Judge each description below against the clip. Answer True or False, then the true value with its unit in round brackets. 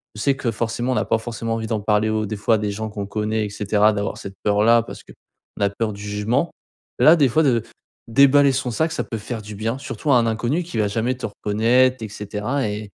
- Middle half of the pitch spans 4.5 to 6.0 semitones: False (3.3 semitones)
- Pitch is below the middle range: True (110 Hz)